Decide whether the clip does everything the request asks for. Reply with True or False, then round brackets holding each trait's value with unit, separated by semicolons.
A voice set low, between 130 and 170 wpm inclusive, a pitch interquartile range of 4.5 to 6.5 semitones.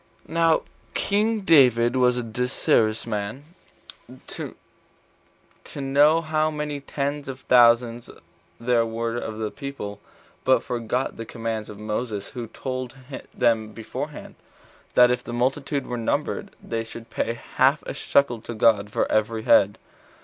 False (120 Hz; 135 wpm; 3.5 semitones)